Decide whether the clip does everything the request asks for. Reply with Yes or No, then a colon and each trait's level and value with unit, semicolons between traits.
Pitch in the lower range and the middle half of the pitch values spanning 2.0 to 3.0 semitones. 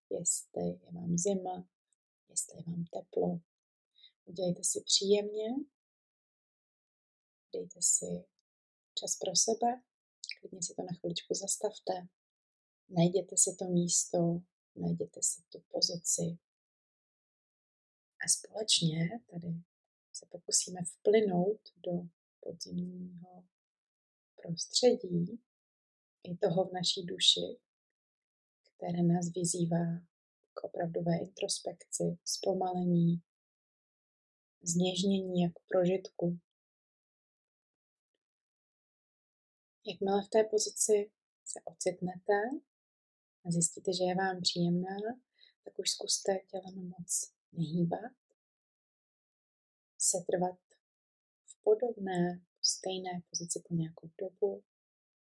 No: medium, 180 Hz; narrow, 2.5 semitones